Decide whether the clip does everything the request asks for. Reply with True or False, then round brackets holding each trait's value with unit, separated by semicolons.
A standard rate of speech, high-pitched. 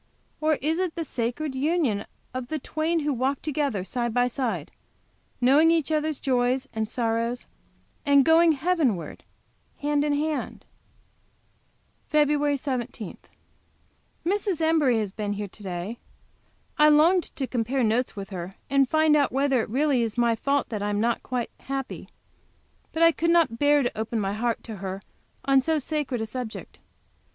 True (160 wpm; 265 Hz)